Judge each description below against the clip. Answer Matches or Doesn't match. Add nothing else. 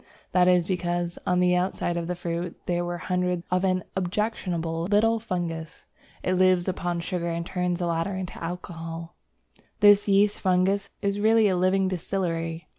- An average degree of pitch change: Doesn't match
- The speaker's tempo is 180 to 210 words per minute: Doesn't match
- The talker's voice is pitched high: Doesn't match